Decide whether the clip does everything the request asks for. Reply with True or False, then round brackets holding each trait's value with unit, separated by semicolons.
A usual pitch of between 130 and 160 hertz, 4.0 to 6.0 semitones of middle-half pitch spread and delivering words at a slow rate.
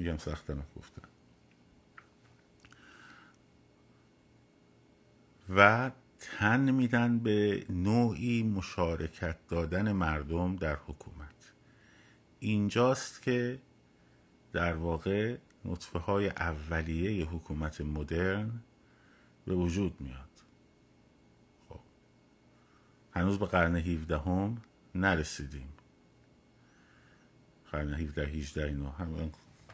False (85 Hz; 5.2 semitones; 75 wpm)